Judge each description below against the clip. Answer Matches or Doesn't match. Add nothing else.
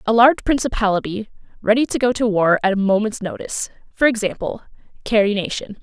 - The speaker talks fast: Doesn't match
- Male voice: Doesn't match